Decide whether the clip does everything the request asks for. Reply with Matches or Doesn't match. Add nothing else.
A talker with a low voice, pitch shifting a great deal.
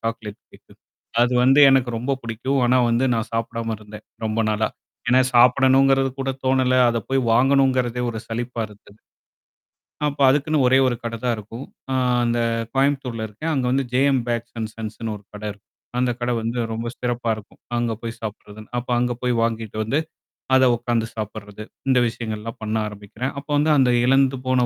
Doesn't match